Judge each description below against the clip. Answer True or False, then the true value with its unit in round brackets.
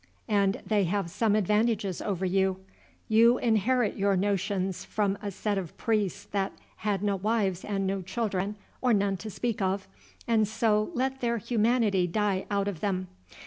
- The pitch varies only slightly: True (2.2 semitones)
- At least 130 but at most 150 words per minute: False (165 wpm)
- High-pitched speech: True (205 Hz)